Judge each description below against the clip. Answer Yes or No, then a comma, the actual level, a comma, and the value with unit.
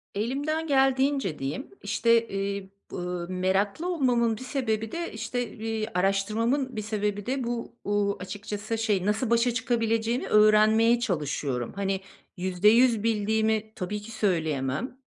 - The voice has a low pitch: No, high, 220 Hz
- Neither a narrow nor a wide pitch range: Yes, average, 3.2 semitones